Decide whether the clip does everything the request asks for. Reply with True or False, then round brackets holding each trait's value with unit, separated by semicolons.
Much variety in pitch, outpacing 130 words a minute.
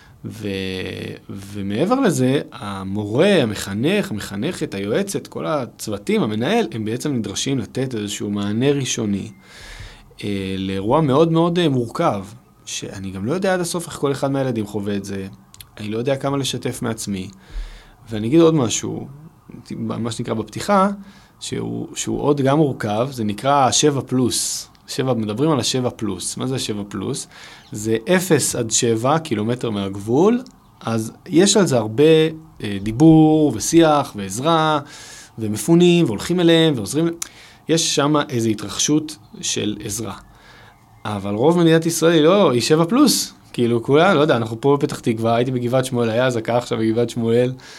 True (5.9 semitones; 145 wpm)